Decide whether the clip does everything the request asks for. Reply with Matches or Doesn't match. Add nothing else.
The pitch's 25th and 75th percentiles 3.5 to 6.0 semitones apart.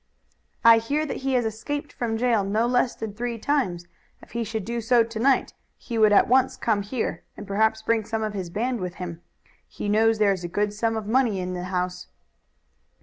Doesn't match